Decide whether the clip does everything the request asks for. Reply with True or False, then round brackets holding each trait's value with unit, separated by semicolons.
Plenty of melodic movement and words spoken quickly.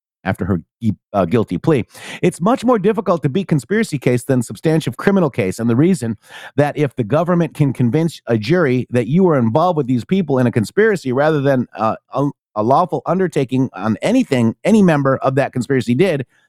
False (6.2 semitones; 195 wpm)